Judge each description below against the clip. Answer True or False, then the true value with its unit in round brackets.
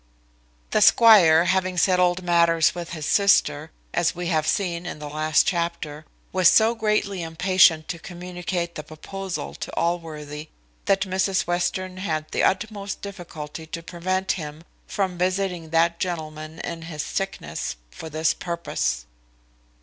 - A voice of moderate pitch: True (170 Hz)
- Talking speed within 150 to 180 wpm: False (140 wpm)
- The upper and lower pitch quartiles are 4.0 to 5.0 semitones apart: False (2.9 semitones)